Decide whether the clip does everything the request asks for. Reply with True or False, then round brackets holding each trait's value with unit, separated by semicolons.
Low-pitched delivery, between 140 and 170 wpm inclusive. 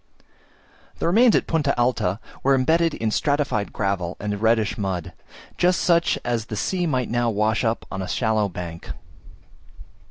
True (115 Hz; 155 wpm)